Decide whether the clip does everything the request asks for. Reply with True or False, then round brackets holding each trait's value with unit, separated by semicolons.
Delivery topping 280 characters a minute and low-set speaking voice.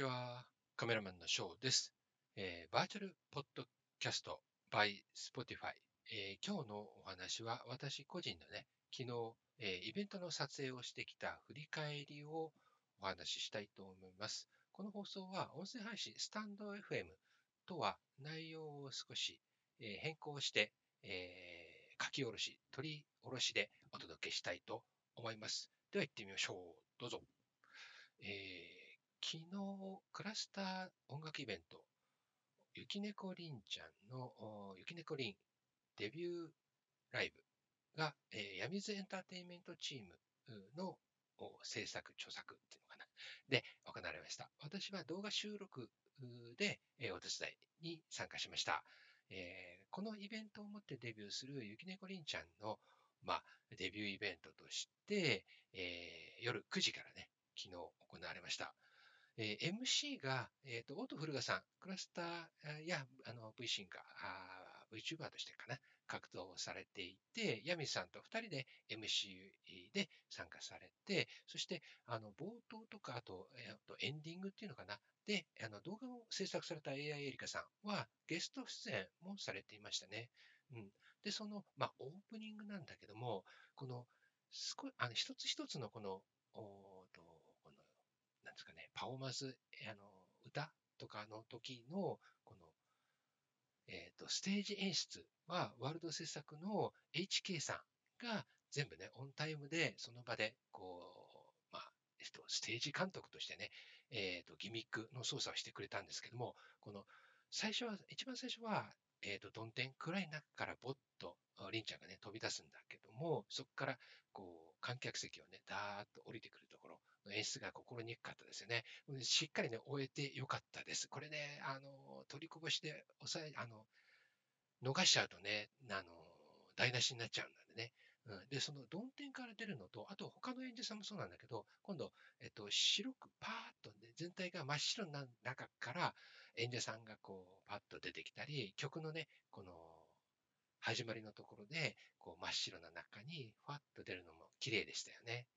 True (315 characters per minute; 130 Hz)